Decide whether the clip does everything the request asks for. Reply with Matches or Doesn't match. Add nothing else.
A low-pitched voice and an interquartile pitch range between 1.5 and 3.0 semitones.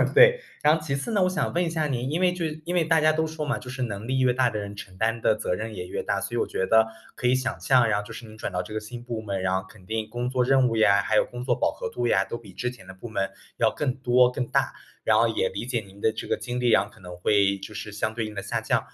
Doesn't match